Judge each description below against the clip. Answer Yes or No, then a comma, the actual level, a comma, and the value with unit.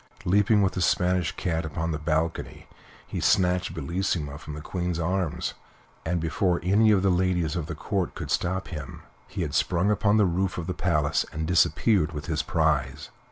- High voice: No, very low, 85 Hz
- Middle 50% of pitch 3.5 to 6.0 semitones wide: No, average, 2.9 semitones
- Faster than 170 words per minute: Yes, average, 185 wpm